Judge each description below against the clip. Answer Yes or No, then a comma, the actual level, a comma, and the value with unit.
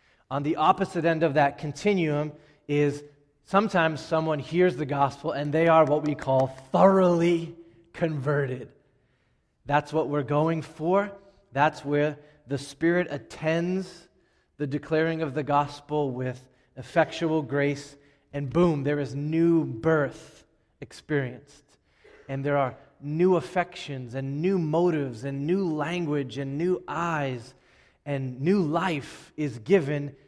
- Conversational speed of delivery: No, slow, 130 wpm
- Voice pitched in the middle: Yes, medium, 150 Hz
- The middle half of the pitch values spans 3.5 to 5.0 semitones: No, average, 2.8 semitones